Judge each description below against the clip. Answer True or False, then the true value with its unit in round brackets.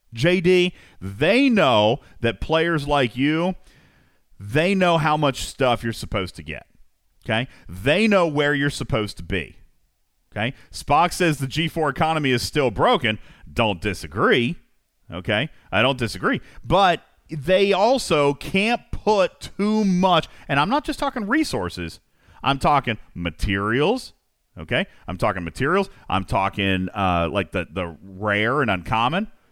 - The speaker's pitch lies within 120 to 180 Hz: True (135 Hz)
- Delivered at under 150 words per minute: True (140 wpm)